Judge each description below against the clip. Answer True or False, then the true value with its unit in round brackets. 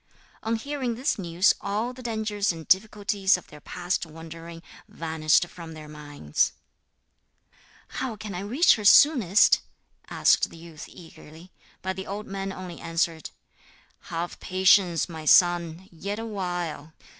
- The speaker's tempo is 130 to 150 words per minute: True (135 wpm)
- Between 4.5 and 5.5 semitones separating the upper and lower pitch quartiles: False (3.9 semitones)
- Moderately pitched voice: True (180 Hz)